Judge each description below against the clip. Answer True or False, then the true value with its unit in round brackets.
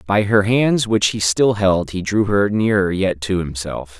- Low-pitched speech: True (100 Hz)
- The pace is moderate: False (210 wpm)